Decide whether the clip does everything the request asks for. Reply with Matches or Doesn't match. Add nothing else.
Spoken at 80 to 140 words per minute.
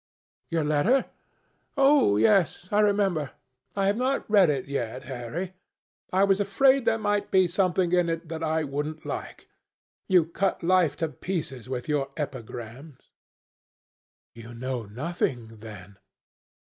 Matches